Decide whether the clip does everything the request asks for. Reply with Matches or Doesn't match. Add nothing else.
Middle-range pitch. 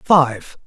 Matches